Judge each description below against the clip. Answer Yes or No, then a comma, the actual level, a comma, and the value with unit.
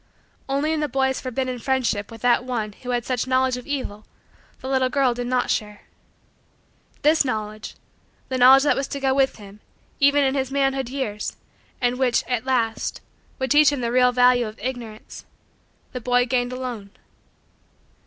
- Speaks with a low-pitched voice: No, very high, 255 Hz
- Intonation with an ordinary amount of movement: No, narrow, 2.0 semitones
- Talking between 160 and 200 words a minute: Yes, average, 175 wpm